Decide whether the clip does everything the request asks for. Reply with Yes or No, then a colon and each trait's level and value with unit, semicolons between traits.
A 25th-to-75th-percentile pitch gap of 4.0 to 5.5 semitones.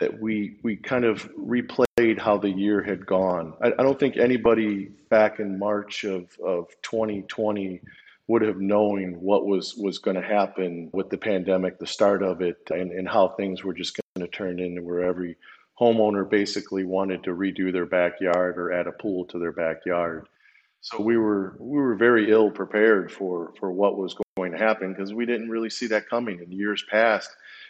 No: average, 3.0 semitones